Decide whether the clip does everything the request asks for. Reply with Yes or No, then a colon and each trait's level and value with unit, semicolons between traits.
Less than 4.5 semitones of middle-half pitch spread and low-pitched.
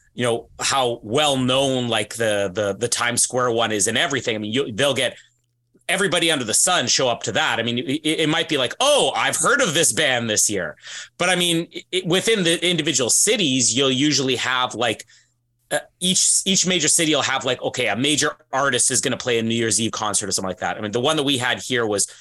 No: average, 5.1 semitones; low, 130 Hz